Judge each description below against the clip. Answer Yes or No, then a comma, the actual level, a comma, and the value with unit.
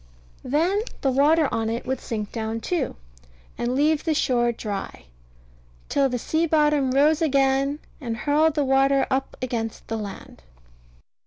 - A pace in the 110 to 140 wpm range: No, average, 155 wpm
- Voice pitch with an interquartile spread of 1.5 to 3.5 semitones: No, average, 4.1 semitones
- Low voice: No, very high, 270 Hz